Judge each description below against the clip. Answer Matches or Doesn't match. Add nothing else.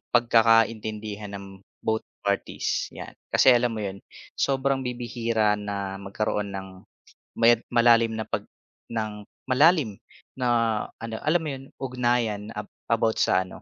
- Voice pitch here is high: Doesn't match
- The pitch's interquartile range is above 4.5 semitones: Doesn't match